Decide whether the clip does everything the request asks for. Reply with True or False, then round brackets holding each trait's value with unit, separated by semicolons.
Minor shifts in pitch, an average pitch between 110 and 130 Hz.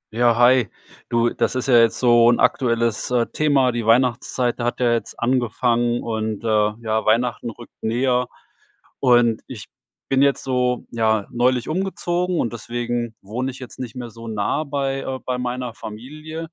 True (1.7 semitones; 120 Hz)